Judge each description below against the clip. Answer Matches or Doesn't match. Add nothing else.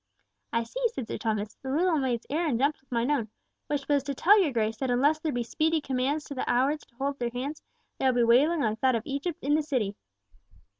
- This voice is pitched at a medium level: Doesn't match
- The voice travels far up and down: Doesn't match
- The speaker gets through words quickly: Matches